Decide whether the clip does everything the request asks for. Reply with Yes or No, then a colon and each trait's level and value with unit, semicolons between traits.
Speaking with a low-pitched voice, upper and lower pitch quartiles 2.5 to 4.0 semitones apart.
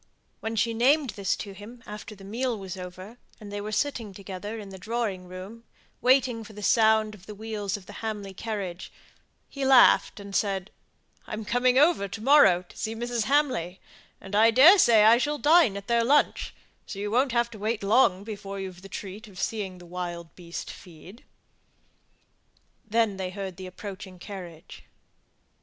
No: high, 210 Hz; average, 3.3 semitones